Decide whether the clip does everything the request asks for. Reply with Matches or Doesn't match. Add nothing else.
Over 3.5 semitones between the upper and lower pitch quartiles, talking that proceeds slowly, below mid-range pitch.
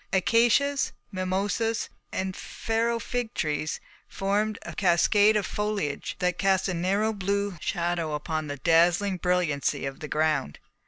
Doesn't match